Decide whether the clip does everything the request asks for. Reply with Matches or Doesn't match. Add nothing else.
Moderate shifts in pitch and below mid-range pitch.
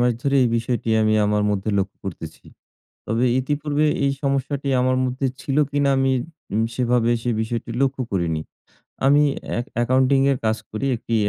Matches